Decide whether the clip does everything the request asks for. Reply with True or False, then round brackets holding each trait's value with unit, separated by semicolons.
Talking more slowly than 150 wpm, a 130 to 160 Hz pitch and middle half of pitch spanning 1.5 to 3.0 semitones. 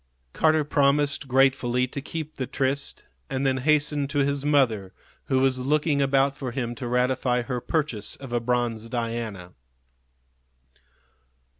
True (140 wpm; 135 Hz; 2.7 semitones)